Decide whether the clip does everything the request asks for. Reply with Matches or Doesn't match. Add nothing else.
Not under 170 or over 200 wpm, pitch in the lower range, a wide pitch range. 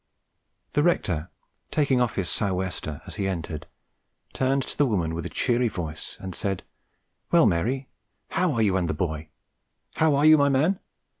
Matches